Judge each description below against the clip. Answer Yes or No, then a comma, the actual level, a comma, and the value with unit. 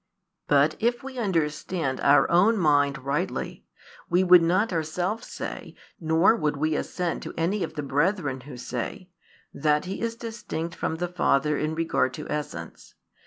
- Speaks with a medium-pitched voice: Yes, medium, 165 Hz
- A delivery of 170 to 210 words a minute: No, average, 160 wpm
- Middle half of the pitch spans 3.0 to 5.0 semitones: Yes, average, 3.9 semitones